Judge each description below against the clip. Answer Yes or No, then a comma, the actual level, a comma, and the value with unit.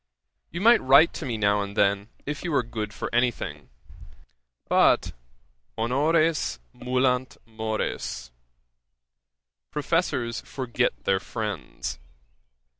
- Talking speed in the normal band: No, slow, 110 wpm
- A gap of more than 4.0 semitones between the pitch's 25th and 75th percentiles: Yes, average, 5.2 semitones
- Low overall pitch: Yes, low, 120 Hz